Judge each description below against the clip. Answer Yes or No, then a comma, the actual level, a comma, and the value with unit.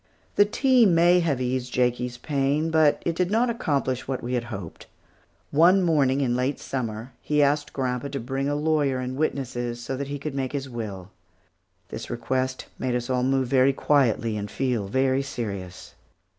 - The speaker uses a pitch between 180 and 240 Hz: No, low, 135 Hz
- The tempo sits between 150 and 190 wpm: Yes, average, 185 wpm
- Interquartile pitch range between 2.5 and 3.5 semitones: Yes, average, 2.9 semitones